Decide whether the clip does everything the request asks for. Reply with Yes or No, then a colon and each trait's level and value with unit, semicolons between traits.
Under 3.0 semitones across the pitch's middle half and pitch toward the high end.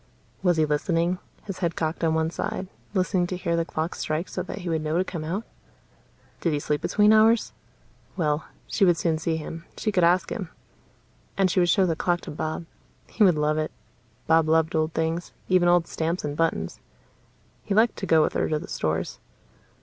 No: narrow, 2.6 semitones; medium, 165 Hz